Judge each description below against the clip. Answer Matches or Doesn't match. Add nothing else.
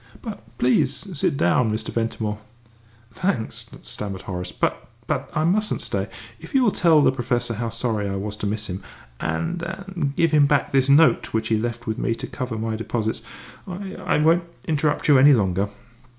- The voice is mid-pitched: Doesn't match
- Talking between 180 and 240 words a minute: Matches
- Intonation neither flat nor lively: Doesn't match